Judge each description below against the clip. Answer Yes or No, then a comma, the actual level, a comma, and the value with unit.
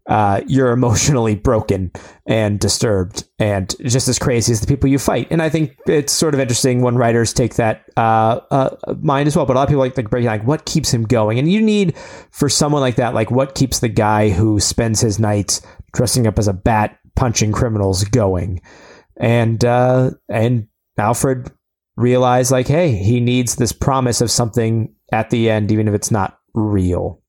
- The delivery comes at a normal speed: Yes, average, 195 wpm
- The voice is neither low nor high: No, low, 120 Hz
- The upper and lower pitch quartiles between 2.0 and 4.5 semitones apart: Yes, average, 3.4 semitones